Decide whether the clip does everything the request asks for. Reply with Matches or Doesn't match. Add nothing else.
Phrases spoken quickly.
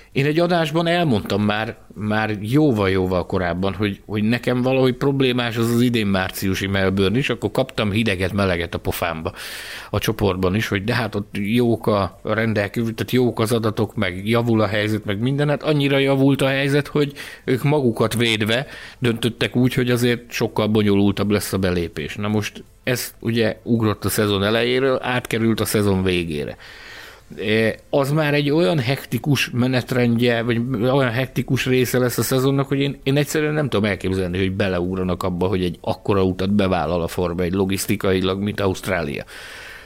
Matches